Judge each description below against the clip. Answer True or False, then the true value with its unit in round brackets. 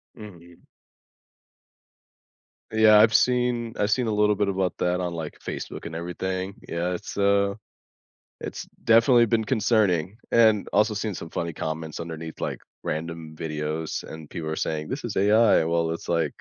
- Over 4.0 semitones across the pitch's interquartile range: True (4.6 semitones)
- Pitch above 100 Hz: False (95 Hz)